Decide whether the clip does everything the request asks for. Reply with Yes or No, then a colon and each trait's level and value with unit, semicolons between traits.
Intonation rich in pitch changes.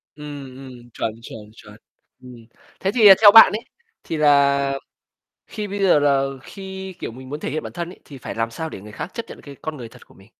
Yes: wide, 6.3 semitones